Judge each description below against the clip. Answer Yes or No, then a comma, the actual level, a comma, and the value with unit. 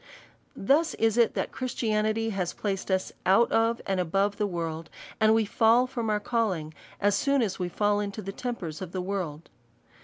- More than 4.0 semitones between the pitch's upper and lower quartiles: No, average, 3.3 semitones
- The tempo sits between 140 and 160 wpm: No, average, 190 wpm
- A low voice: No, high, 205 Hz